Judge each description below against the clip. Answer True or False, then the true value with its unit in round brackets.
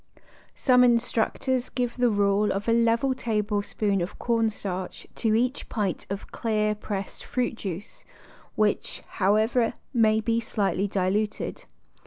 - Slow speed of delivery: True (130 wpm)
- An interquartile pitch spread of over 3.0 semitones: False (2.5 semitones)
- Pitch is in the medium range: False (215 Hz)